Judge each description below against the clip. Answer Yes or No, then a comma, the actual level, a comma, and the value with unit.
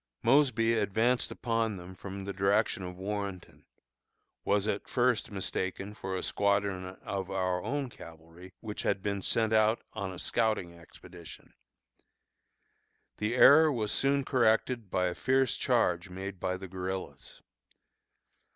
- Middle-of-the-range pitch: No, low, 100 Hz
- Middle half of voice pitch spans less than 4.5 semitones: Yes, average, 3.5 semitones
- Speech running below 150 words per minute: Yes, slow, 135 wpm